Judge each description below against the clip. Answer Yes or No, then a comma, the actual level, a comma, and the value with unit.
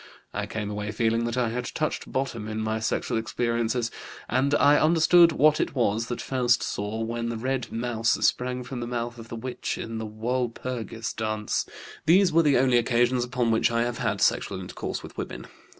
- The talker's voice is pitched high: No, low, 120 Hz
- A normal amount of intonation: No, narrow, 2.2 semitones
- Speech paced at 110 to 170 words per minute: No, average, 195 wpm